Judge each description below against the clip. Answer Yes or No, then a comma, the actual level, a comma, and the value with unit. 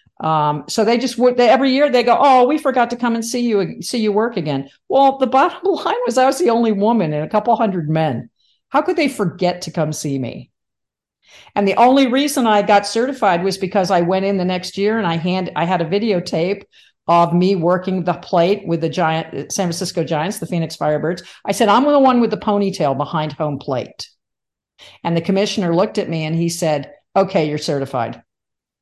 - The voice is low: No, high, 190 Hz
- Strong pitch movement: Yes, wide, 5.9 semitones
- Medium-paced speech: No, fast, 215 wpm